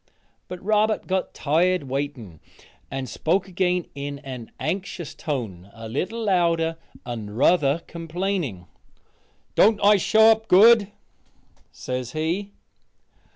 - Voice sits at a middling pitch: Yes, medium, 170 Hz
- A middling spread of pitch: No, wide, 6.4 semitones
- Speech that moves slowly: Yes, slow, 110 wpm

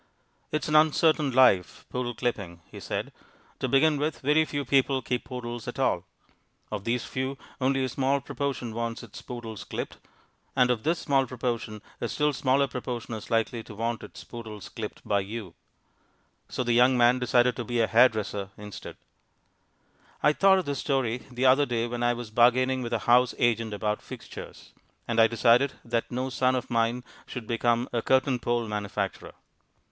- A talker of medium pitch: No, low, 120 Hz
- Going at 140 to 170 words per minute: No, average, 185 wpm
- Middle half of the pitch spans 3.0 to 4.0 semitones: No, narrow, 2.4 semitones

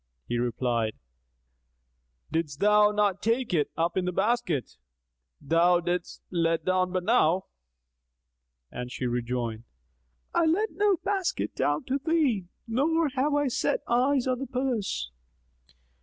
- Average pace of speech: No, slow, 130 wpm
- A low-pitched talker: No, high, 200 Hz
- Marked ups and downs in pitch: Yes, wide, 8.1 semitones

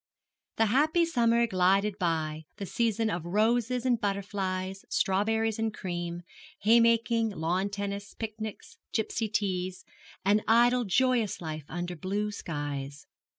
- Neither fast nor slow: No, slow, 120 wpm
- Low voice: No, high, 205 Hz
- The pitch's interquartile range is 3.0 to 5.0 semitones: Yes, average, 3.8 semitones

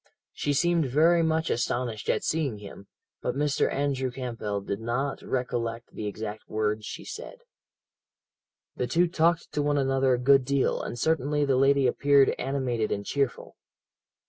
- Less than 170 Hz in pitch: Yes, low, 135 Hz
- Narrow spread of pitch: No, average, 3.6 semitones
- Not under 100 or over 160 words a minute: Yes, average, 155 wpm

